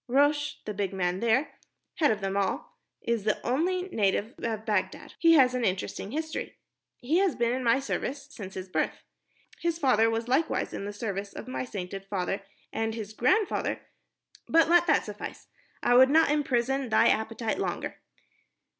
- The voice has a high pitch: Yes, high, 235 Hz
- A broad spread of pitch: Yes, wide, 5.8 semitones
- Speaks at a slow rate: No, average, 170 wpm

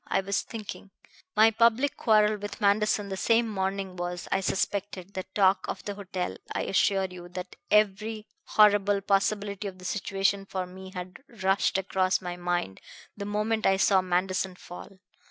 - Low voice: No, high, 195 Hz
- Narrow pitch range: Yes, narrow, 1.9 semitones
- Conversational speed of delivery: Yes, average, 165 wpm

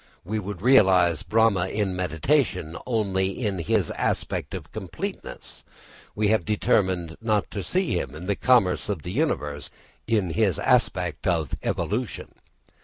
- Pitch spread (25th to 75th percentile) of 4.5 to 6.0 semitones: No, average, 3.7 semitones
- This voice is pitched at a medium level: No, very low, 95 Hz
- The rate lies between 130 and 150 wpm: Yes, average, 140 wpm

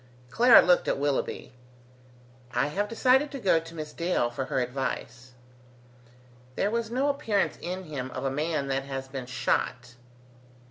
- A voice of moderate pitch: Yes, medium, 150 Hz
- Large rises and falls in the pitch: Yes, wide, 7.4 semitones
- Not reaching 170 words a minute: Yes, average, 155 wpm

